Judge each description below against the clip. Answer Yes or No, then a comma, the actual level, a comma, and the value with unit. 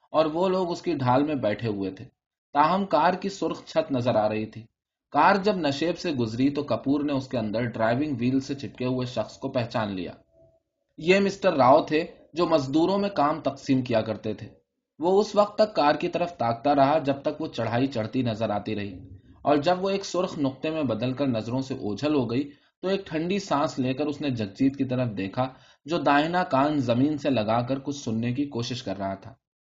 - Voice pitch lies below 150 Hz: Yes, low, 135 Hz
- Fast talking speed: Yes, fast, 215 wpm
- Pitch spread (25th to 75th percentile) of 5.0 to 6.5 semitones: Yes, average, 5.3 semitones